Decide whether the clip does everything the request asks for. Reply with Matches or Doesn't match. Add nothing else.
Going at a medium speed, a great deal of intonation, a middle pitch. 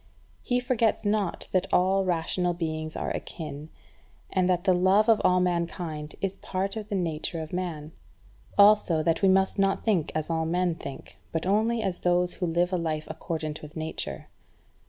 Doesn't match